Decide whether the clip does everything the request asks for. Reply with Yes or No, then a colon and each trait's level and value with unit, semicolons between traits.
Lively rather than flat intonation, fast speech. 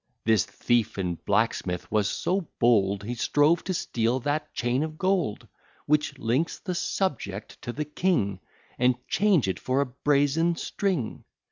No: wide, 6.3 semitones; average, 150 wpm